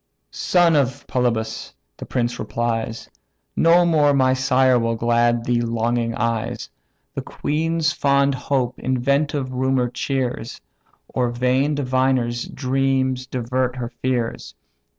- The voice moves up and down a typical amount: No, narrow, 2.2 semitones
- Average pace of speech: No, slow, 120 wpm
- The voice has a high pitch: No, low, 130 Hz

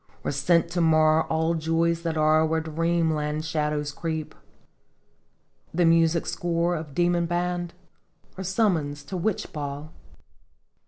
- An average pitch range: No, narrow, 1.8 semitones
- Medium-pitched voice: Yes, medium, 160 Hz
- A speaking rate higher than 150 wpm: No, average, 145 wpm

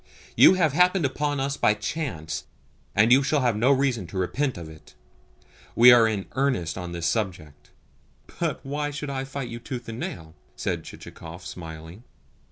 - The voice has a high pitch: No, low, 120 Hz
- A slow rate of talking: No, average, 175 wpm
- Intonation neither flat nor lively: No, wide, 7.8 semitones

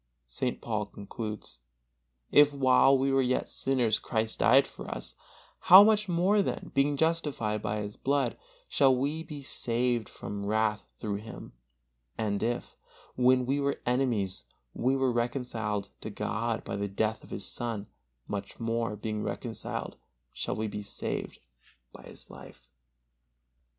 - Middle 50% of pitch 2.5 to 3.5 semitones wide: No, average, 4.2 semitones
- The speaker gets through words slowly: No, average, 145 wpm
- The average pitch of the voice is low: Yes, low, 120 Hz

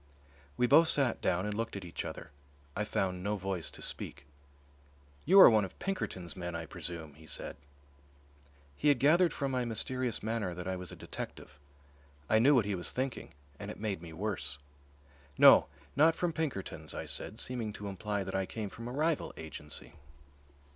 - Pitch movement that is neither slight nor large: No, wide, 6.0 semitones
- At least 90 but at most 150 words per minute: No, average, 185 wpm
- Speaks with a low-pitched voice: Yes, low, 105 Hz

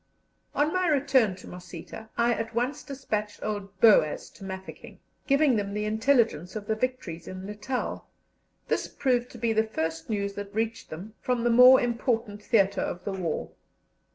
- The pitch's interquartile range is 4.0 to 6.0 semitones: No, average, 3.6 semitones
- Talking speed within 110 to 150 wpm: No, average, 170 wpm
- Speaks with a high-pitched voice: Yes, high, 220 Hz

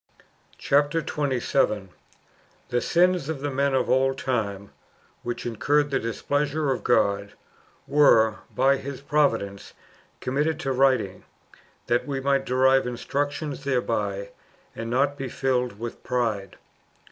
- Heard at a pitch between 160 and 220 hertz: No, low, 130 Hz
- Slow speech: Yes, slow, 125 wpm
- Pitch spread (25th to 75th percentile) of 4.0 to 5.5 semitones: No, average, 3.6 semitones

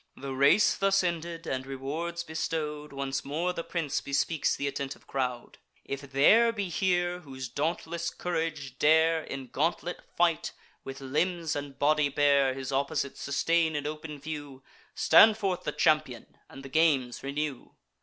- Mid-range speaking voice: Yes, medium, 150 Hz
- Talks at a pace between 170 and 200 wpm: No, average, 150 wpm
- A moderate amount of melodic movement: Yes, average, 3.3 semitones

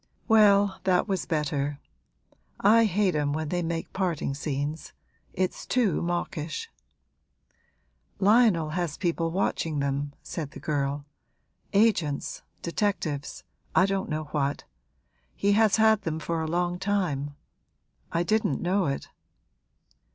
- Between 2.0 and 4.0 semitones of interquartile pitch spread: No, average, 4.9 semitones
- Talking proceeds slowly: Yes, slow, 120 wpm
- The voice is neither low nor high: Yes, medium, 170 Hz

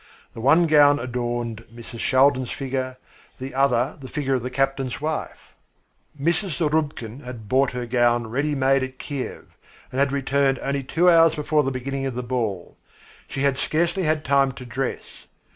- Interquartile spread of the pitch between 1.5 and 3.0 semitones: Yes, narrow, 2.5 semitones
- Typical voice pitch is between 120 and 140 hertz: Yes, low, 135 Hz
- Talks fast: No, average, 170 wpm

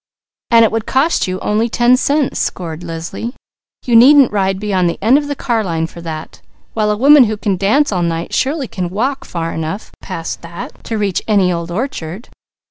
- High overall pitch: Yes, high, 210 Hz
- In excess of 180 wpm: Yes, average, 190 wpm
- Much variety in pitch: Yes, wide, 5.9 semitones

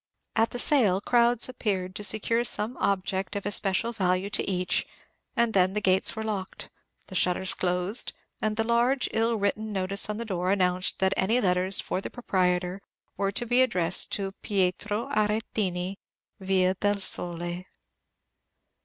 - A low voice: No, high, 200 Hz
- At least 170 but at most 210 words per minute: No, average, 155 wpm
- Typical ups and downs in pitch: Yes, average, 3.0 semitones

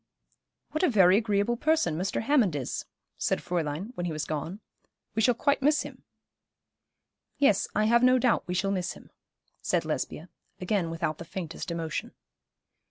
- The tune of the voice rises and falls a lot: Yes, wide, 6.0 semitones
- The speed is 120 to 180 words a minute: Yes, average, 165 wpm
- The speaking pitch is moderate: No, high, 195 Hz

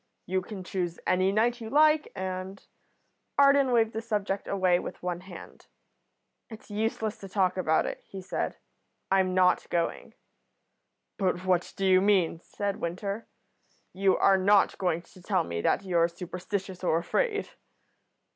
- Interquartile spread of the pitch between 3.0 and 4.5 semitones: No, narrow, 2.5 semitones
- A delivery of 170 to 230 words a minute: No, average, 155 wpm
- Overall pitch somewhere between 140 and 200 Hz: Yes, high, 190 Hz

